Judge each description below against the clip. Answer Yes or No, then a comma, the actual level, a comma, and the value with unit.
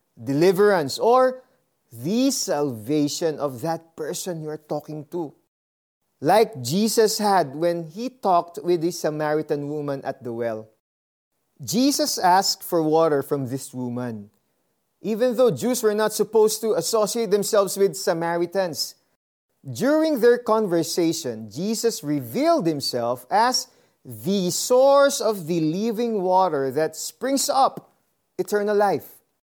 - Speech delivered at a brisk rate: No, average, 120 wpm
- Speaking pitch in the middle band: Yes, medium, 175 Hz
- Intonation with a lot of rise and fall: Yes, wide, 7.0 semitones